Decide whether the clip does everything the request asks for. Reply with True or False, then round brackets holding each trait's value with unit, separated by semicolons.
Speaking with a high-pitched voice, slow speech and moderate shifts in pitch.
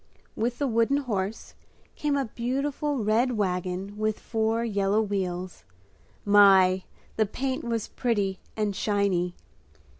True (215 Hz; 120 wpm; 3.5 semitones)